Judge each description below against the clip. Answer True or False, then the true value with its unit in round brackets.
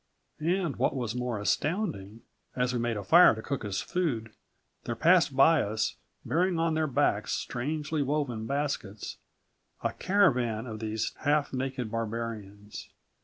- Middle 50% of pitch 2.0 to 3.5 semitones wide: False (5.6 semitones)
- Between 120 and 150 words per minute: True (145 wpm)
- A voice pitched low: True (125 Hz)